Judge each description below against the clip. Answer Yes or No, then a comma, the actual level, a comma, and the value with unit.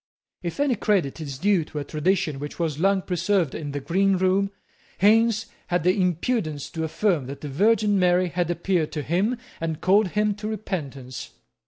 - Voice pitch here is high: No, medium, 180 Hz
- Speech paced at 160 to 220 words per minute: Yes, average, 180 wpm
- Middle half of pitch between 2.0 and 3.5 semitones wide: No, average, 4.7 semitones